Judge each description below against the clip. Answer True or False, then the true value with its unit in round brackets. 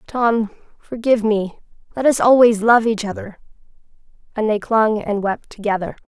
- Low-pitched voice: False (220 Hz)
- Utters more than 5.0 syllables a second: False (4.9 syllables/s)